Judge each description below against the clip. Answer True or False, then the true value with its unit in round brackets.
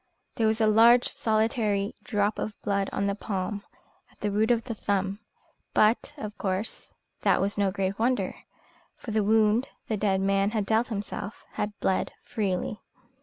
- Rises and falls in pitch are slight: True (1.9 semitones)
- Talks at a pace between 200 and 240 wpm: False (170 wpm)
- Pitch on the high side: True (210 Hz)